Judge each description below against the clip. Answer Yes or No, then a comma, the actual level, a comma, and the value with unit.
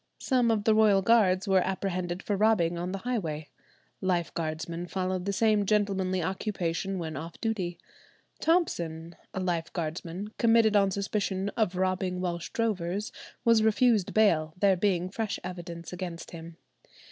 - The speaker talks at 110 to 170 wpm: Yes, average, 140 wpm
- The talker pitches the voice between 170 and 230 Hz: Yes, medium, 185 Hz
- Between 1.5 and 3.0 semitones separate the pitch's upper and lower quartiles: No, average, 3.4 semitones